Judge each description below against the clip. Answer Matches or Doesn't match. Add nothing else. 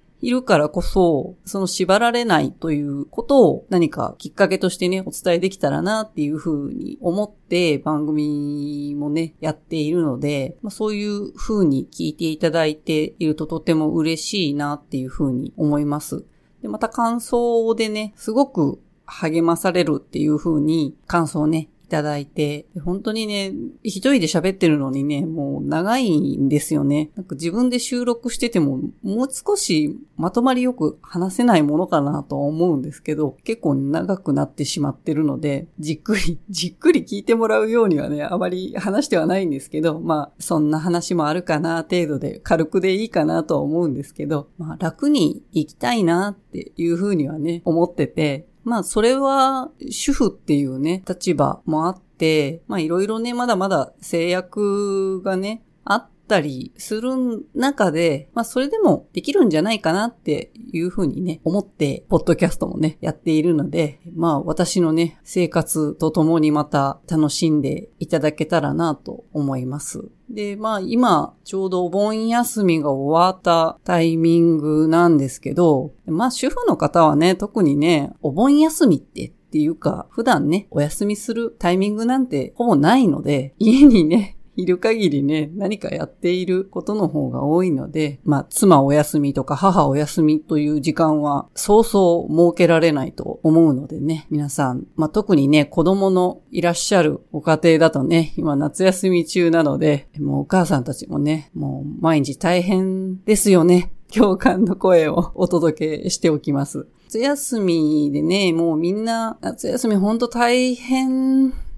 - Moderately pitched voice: Matches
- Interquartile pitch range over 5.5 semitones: Doesn't match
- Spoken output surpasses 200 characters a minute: Matches